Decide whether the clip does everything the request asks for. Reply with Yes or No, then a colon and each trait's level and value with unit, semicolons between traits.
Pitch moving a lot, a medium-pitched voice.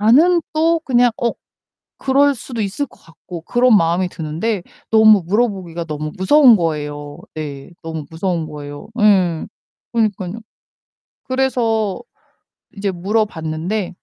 No: wide, 6.3 semitones; high, 195 Hz